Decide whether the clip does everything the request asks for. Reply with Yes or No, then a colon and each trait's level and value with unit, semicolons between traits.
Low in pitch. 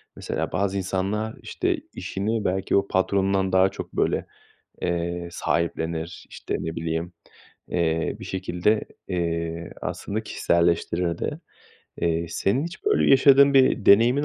Yes: very low, 95 Hz